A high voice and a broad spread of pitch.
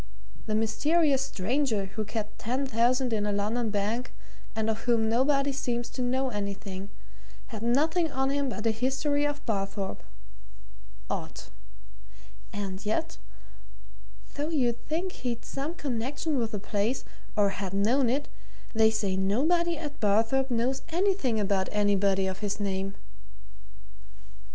No: high, 230 Hz; average, 4.8 semitones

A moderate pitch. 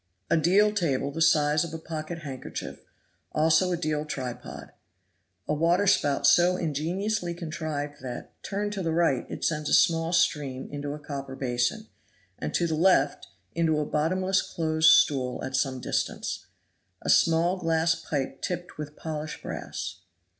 Yes: medium, 155 Hz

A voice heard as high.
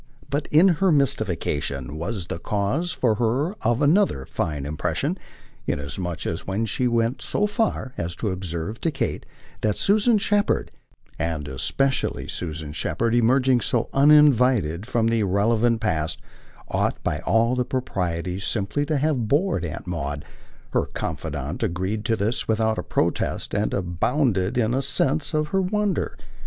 No: low, 115 Hz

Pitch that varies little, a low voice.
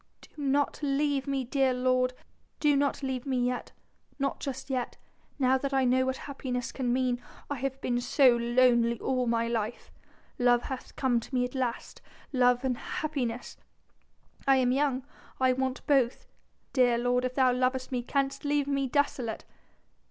No: narrow, 1.7 semitones; very high, 255 Hz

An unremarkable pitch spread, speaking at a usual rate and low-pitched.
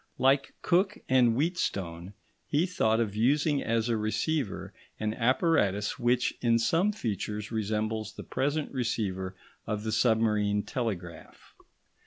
No: average, 4.2 semitones; slow, 125 wpm; low, 115 Hz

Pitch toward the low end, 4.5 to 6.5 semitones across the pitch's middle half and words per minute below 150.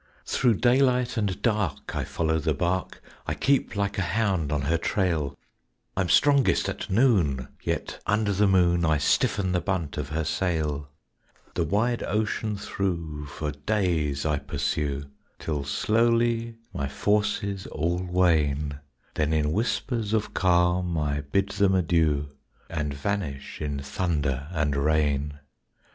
Yes: very low, 85 Hz; wide, 5.5 semitones; average, 140 wpm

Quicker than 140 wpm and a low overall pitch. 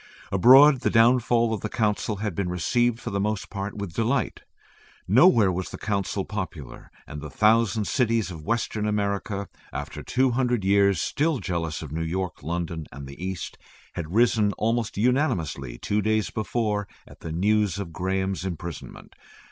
Yes: average, 165 wpm; low, 100 Hz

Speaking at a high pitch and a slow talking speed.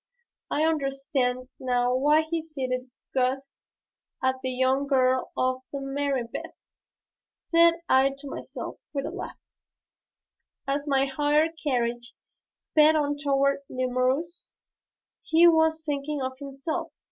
Yes: very high, 275 Hz; slow, 115 wpm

